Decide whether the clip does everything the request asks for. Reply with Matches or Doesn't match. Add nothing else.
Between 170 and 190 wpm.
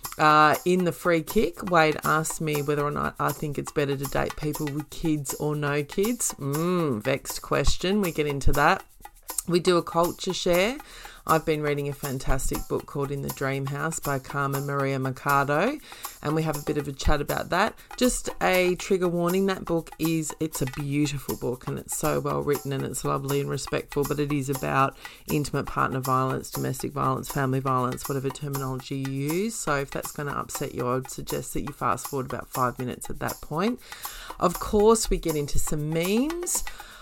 Doesn't match